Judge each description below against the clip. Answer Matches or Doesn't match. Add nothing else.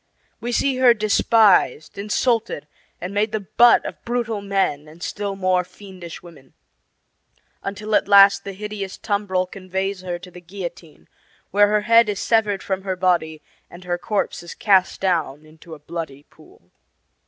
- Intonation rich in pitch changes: Doesn't match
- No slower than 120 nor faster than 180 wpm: Matches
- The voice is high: Matches